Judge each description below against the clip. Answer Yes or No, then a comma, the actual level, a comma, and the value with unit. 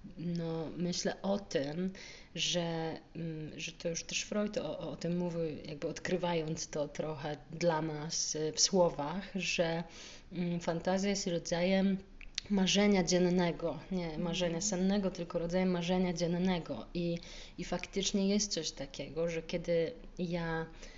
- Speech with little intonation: Yes, narrow, 2.1 semitones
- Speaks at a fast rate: No, average, 125 wpm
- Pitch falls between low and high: Yes, medium, 175 Hz